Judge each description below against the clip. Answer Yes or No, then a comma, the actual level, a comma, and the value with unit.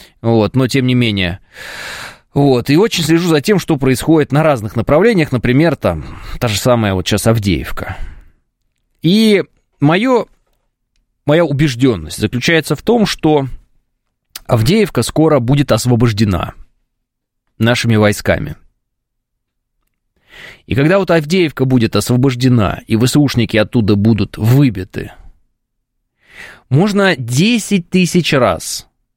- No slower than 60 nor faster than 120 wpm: Yes, slow, 110 wpm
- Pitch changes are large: Yes, wide, 5.8 semitones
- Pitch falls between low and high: No, low, 130 Hz